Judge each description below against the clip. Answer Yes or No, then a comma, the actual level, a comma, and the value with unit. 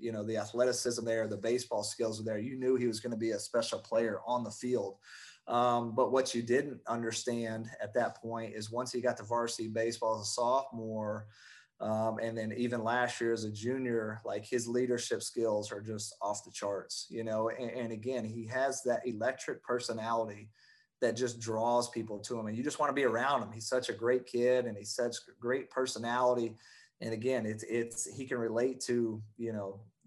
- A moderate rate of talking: No, fast, 210 wpm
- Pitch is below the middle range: Yes, low, 115 Hz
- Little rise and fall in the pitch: Yes, narrow, 1.8 semitones